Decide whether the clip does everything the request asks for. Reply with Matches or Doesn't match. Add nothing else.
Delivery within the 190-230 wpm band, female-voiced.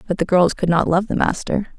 Doesn't match